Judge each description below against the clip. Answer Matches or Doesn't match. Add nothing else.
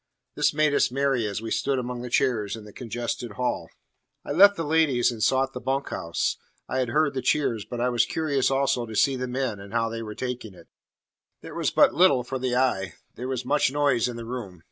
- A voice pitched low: Matches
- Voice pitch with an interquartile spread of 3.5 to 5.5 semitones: Doesn't match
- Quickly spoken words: Matches